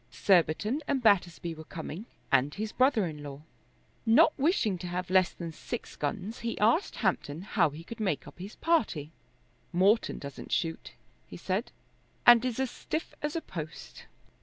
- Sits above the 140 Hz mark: Yes, high, 190 Hz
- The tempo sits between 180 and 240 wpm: No, average, 165 wpm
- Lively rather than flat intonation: Yes, wide, 6.2 semitones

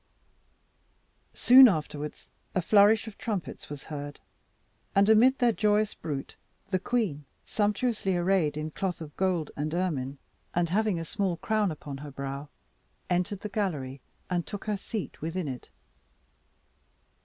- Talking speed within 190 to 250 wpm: No, average, 140 wpm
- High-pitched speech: No, medium, 180 Hz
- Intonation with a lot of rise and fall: Yes, wide, 5.7 semitones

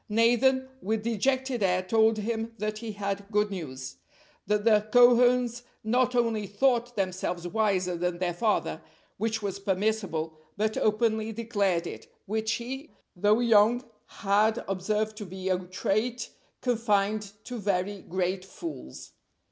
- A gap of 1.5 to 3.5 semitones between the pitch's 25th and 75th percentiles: Yes, average, 3.0 semitones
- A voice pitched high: Yes, high, 215 Hz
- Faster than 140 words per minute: No, slow, 135 wpm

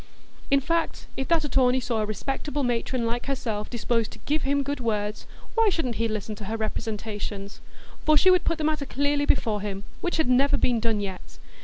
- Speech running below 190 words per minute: No, average, 200 wpm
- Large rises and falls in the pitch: No, average, 4.9 semitones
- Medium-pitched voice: No, very high, 250 Hz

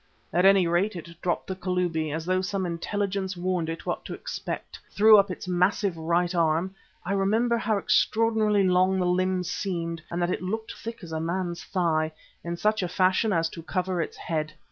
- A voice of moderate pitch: Yes, medium, 180 Hz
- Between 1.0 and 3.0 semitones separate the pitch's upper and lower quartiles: Yes, narrow, 2.5 semitones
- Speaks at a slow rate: No, average, 200 wpm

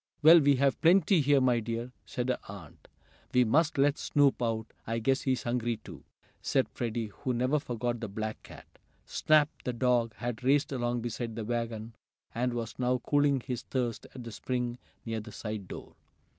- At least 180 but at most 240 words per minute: Yes, average, 185 wpm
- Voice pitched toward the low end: Yes, low, 120 Hz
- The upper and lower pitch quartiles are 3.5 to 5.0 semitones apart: No, average, 2.7 semitones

